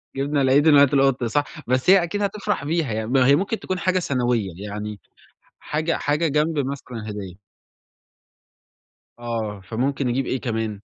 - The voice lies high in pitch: No, low, 135 Hz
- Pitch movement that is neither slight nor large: Yes, average, 5.0 semitones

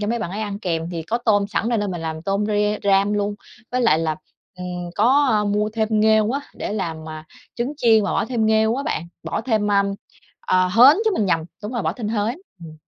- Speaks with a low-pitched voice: No, high, 210 Hz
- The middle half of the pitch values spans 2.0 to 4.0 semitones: Yes, average, 3.5 semitones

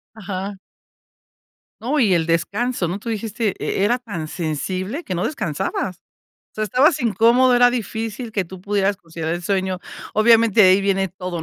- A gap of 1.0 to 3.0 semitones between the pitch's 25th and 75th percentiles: No, average, 3.9 semitones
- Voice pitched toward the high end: Yes, high, 200 Hz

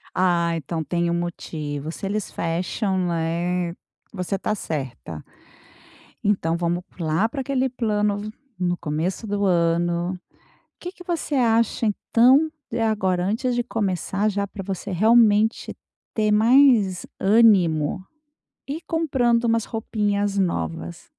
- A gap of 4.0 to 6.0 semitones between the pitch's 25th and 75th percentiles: Yes, average, 4.7 semitones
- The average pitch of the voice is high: Yes, high, 195 Hz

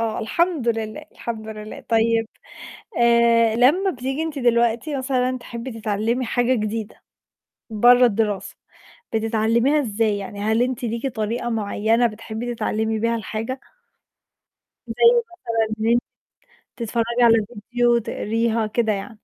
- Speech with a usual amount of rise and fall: No, narrow, 1.9 semitones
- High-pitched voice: Yes, high, 230 Hz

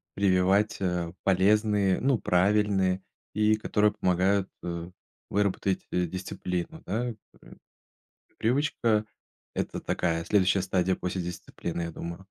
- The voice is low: Yes, very low, 95 Hz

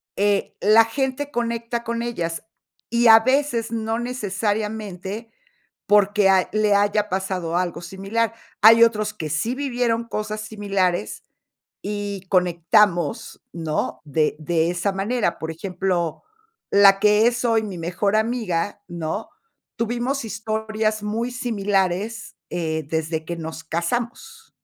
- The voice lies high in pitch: Yes, high, 210 Hz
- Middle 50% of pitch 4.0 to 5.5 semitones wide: Yes, average, 4.3 semitones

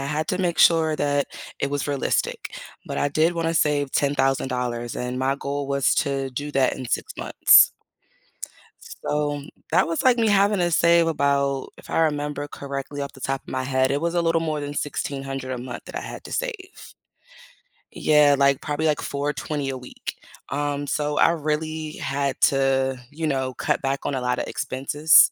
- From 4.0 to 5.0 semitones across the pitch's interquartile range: No, narrow, 2.4 semitones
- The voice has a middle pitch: Yes, medium, 145 Hz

